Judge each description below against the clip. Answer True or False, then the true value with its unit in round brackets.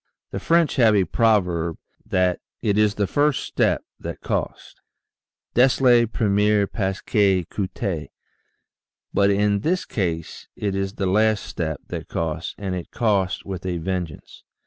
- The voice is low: True (100 Hz)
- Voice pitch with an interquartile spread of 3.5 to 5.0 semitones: False (2.9 semitones)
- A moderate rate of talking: True (150 wpm)